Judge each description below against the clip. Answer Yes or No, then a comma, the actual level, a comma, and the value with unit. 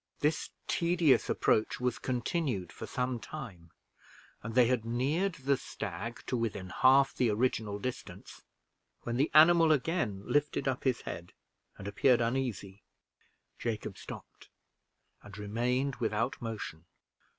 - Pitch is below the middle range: Yes, low, 125 Hz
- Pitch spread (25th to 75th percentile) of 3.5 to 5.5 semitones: Yes, average, 4.3 semitones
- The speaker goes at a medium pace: No, slow, 130 wpm